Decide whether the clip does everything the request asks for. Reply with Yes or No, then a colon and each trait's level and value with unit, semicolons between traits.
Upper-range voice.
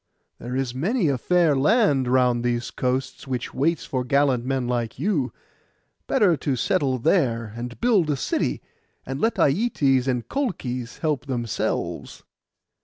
No: low, 135 Hz